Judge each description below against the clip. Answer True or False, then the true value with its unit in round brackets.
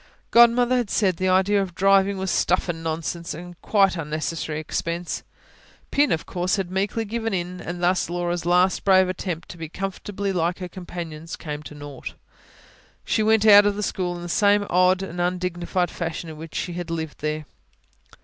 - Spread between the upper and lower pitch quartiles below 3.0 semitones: True (2.6 semitones)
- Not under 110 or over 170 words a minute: False (185 wpm)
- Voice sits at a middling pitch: True (180 Hz)